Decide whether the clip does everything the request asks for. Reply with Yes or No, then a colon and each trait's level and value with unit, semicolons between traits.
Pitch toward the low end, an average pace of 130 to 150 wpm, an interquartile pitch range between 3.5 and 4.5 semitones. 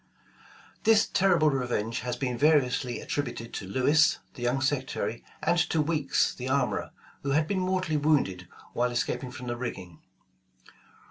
Yes: low, 130 Hz; average, 145 wpm; average, 4.1 semitones